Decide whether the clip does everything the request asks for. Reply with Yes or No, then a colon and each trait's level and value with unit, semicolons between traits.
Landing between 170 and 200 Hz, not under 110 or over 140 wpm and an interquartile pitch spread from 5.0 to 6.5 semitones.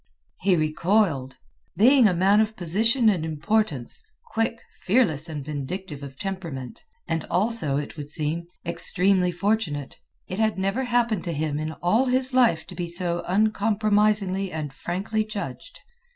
Yes: medium, 185 Hz; slow, 135 wpm; wide, 5.5 semitones